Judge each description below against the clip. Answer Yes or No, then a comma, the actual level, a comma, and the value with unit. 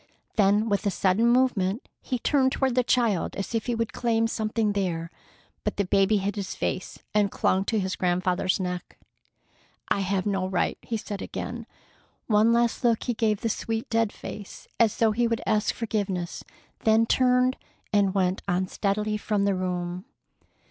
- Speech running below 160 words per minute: No, average, 170 wpm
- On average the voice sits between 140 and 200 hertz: No, high, 210 Hz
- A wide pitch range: No, average, 3.1 semitones